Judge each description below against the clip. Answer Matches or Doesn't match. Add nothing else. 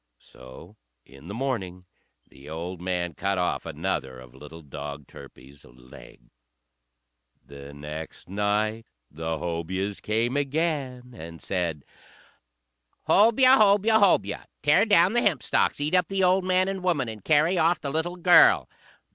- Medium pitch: Doesn't match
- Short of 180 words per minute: Matches